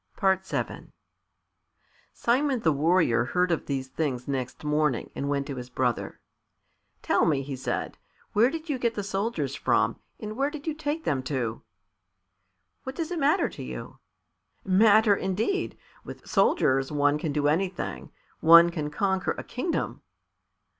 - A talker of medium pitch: Yes, medium, 170 Hz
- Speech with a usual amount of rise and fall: No, wide, 8.3 semitones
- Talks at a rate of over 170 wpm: No, average, 150 wpm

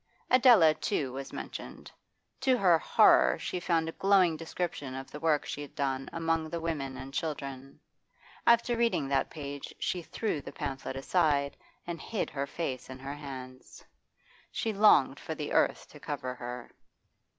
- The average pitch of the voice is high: No, medium, 150 Hz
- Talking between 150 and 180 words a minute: Yes, average, 160 wpm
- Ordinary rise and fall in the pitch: Yes, average, 4.0 semitones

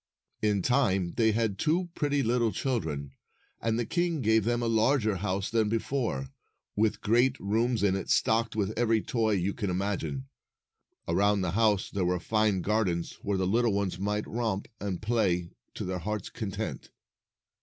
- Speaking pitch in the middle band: No, low, 105 Hz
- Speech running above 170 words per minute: No, average, 165 wpm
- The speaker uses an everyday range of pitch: Yes, average, 3.3 semitones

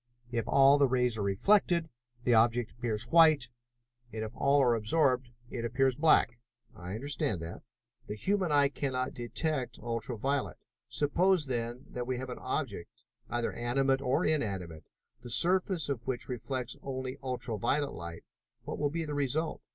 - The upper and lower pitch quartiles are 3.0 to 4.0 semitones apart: Yes, average, 3.6 semitones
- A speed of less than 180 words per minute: Yes, average, 160 wpm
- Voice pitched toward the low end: Yes, low, 130 Hz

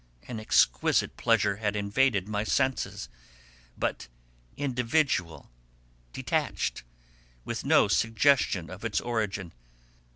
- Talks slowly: Yes, slow, 95 wpm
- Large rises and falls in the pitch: No, average, 3.7 semitones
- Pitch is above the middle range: No, low, 110 Hz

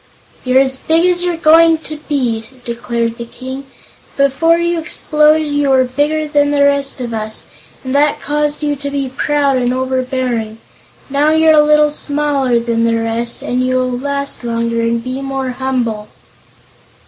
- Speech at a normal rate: Yes, average, 170 wpm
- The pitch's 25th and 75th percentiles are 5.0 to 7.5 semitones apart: No, average, 3.3 semitones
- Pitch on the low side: No, very high, 270 Hz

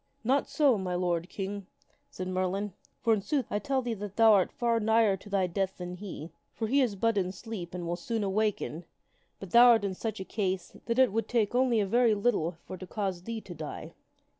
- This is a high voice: Yes, high, 205 Hz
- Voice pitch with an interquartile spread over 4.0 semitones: No, average, 3.7 semitones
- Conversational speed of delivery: No, fast, 240 wpm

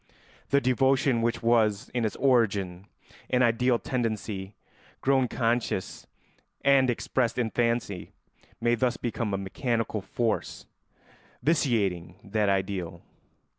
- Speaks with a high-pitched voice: No, low, 115 Hz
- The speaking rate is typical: No, slow, 110 wpm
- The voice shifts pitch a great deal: No, average, 3.7 semitones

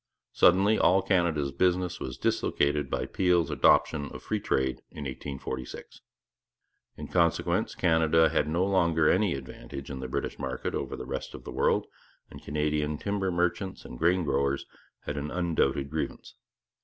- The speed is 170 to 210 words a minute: No, average, 155 wpm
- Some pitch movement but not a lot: Yes, average, 4.3 semitones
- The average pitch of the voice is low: Yes, very low, 80 Hz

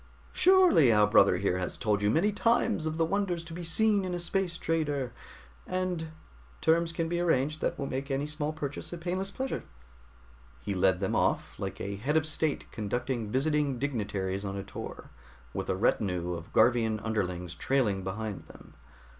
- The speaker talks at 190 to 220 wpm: No, average, 180 wpm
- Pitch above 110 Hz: Yes, medium, 140 Hz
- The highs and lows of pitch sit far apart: Yes, wide, 8.5 semitones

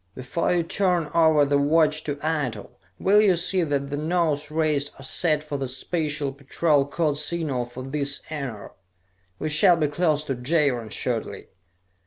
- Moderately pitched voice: Yes, medium, 150 Hz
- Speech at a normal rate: Yes, average, 165 wpm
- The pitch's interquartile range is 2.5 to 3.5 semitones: Yes, average, 2.8 semitones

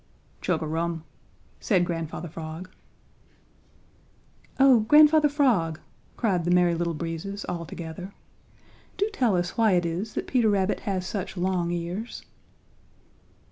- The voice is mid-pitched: Yes, medium, 180 Hz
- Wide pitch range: No, average, 4.2 semitones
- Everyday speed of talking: No, slow, 130 wpm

